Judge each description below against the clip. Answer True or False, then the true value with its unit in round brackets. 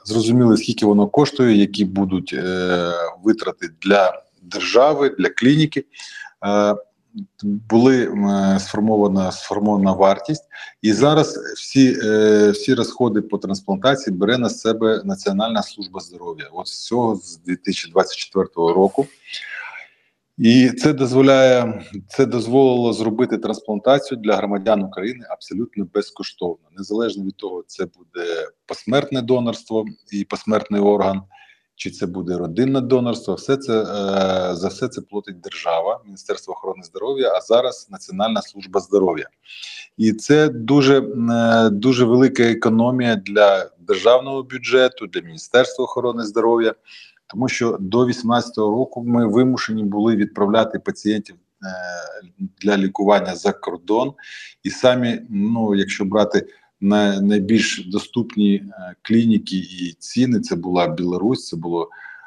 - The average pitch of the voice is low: True (110 Hz)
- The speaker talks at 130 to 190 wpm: False (120 wpm)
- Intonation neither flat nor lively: True (4.3 semitones)